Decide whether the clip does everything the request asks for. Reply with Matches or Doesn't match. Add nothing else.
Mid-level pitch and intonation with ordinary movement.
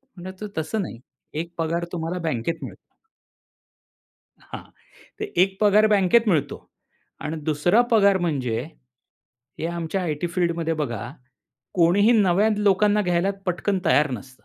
Matches